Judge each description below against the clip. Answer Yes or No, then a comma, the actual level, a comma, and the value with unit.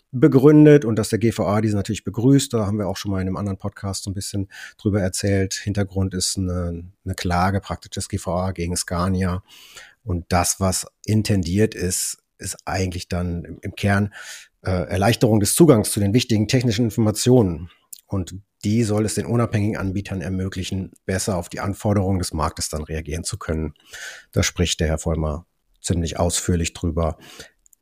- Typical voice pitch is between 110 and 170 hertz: No, very low, 95 Hz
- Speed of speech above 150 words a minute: Yes, average, 170 wpm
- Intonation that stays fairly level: No, average, 3.1 semitones